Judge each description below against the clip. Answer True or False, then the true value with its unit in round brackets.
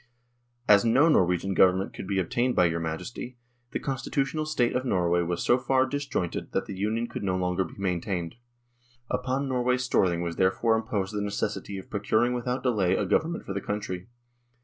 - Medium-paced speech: True (190 wpm)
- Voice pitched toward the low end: True (105 Hz)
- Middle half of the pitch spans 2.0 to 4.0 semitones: False (5.3 semitones)